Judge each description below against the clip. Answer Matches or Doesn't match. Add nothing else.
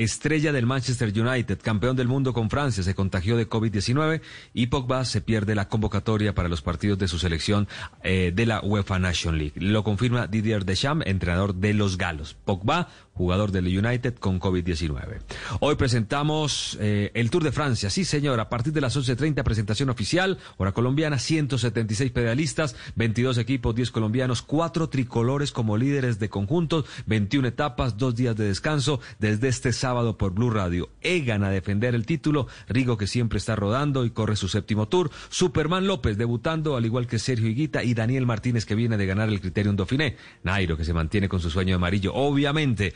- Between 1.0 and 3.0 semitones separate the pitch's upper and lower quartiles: Doesn't match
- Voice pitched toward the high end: Doesn't match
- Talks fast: Doesn't match